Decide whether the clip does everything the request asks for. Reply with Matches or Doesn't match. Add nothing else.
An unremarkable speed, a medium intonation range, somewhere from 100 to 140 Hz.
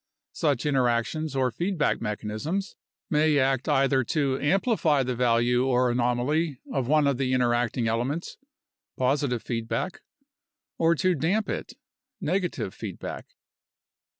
Doesn't match